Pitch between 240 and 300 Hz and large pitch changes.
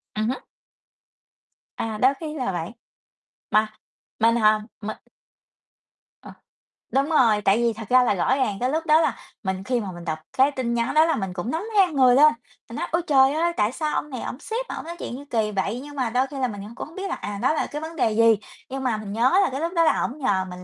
Yes: very high, 250 Hz; wide, 5.8 semitones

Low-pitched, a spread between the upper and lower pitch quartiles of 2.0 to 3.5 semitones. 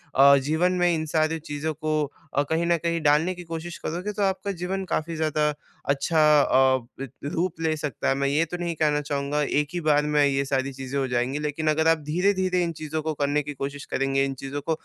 No: medium, 155 Hz; average, 2.8 semitones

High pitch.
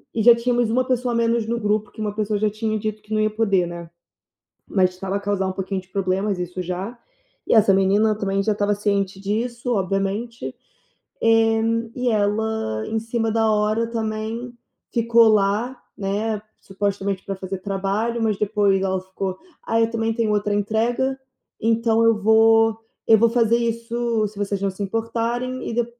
Yes: high, 215 Hz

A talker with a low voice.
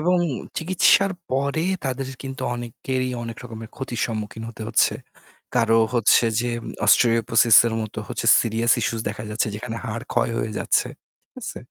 Yes: low, 115 Hz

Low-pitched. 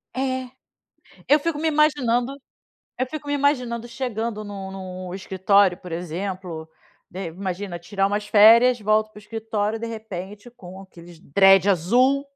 No: high, 210 Hz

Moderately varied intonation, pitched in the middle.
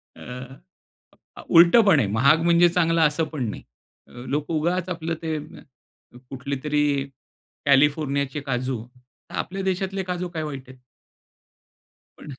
Yes: average, 3.9 semitones; medium, 150 Hz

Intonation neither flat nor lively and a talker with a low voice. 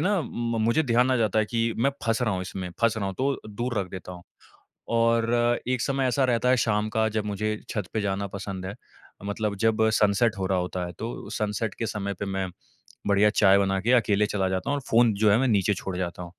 Yes: average, 3.1 semitones; low, 110 Hz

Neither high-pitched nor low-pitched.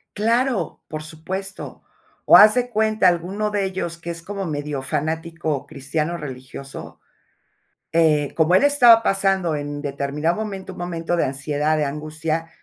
Yes: medium, 165 Hz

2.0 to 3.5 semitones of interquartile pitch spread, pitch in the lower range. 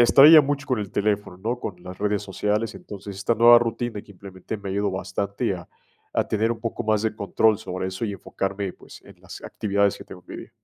Yes: average, 2.7 semitones; low, 105 Hz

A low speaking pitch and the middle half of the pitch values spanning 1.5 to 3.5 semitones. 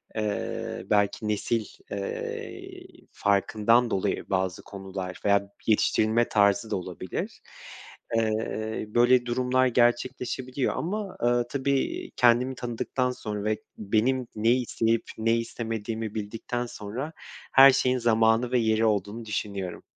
Yes: low, 115 Hz; average, 2.8 semitones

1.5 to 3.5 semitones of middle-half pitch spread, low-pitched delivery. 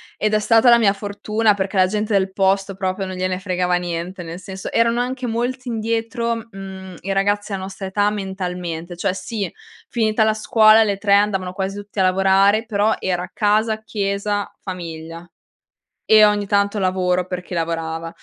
No: narrow, 2.6 semitones; high, 195 Hz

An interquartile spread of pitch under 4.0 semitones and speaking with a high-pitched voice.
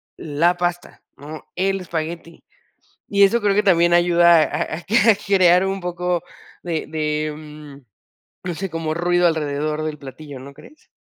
No: narrow, 2.6 semitones; medium, 170 Hz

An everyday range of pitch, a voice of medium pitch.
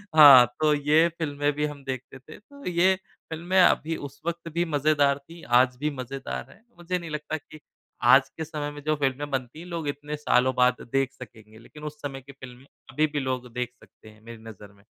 Yes: average, 3.4 semitones; medium, 145 Hz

